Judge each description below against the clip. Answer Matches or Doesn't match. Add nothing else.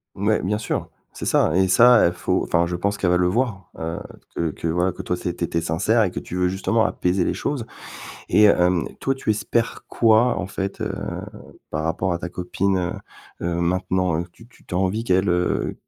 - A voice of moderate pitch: Doesn't match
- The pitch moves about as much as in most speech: Matches